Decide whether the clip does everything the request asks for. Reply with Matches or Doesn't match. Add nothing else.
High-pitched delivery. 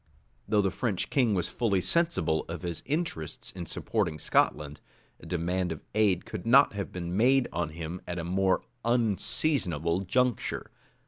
Doesn't match